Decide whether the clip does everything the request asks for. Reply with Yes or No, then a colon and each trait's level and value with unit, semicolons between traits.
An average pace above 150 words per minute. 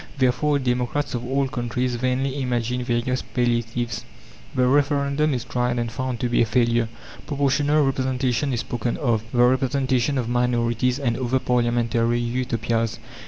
No: average, 145 wpm